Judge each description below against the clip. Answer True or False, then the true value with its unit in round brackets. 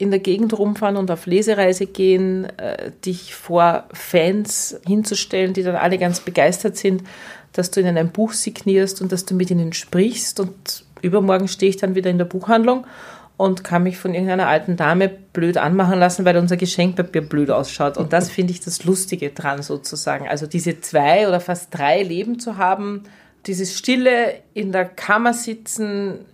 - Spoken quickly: False (175 wpm)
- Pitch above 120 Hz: True (185 Hz)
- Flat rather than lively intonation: True (2.2 semitones)